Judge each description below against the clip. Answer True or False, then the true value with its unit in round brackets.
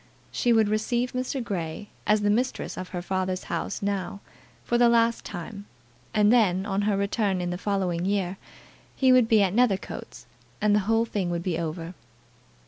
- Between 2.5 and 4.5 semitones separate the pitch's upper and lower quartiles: True (3.5 semitones)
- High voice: True (200 Hz)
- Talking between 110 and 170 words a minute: False (180 wpm)